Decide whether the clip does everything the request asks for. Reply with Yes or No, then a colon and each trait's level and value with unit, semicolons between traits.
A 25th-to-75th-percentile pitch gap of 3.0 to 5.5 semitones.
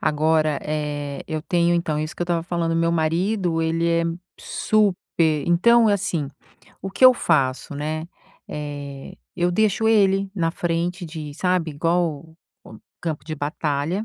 No: narrow, 2.6 semitones